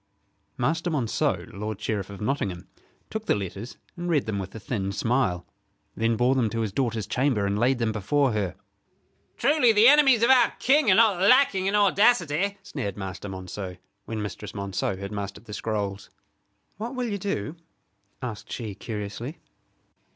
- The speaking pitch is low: Yes, low, 115 Hz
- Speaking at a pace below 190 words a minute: Yes, average, 165 wpm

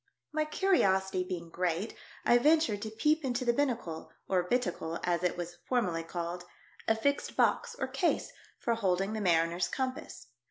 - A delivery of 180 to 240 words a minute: No, average, 170 wpm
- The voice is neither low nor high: No, high, 195 Hz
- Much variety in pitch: Yes, wide, 6.0 semitones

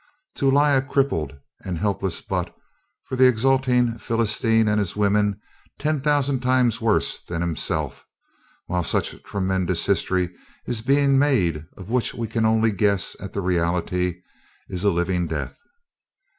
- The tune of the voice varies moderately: No, wide, 5.8 semitones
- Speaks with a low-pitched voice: Yes, low, 105 Hz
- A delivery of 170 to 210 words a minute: No, average, 145 wpm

